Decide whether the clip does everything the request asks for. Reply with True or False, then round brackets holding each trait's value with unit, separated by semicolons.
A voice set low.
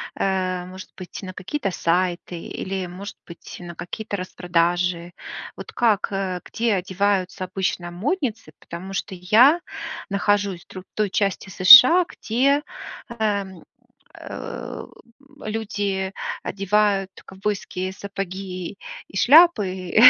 False (190 Hz)